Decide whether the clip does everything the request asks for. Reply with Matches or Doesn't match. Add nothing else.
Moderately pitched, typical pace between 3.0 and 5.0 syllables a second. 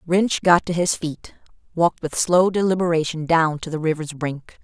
Matches